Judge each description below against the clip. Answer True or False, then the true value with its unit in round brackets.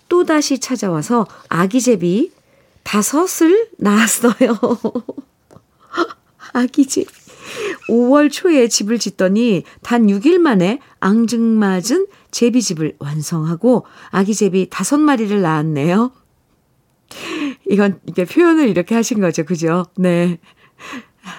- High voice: True (230 Hz)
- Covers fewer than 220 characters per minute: True (210 characters per minute)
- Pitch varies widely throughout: True (6.9 semitones)